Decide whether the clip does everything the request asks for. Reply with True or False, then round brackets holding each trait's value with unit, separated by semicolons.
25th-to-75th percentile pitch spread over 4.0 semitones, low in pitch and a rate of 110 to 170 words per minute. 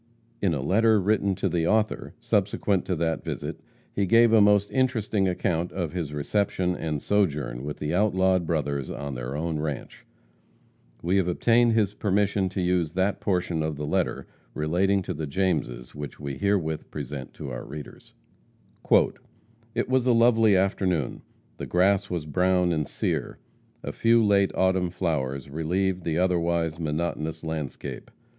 True (4.4 semitones; 90 Hz; 155 wpm)